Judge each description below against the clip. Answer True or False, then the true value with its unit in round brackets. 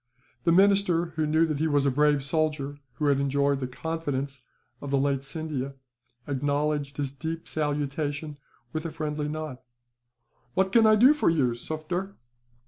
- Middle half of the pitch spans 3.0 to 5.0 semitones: False (2.4 semitones)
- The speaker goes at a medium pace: True (160 wpm)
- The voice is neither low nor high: True (150 Hz)